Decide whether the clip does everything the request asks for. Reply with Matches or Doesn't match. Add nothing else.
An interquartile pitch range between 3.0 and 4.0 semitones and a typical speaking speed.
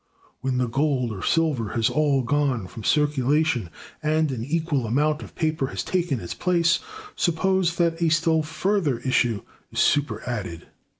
Doesn't match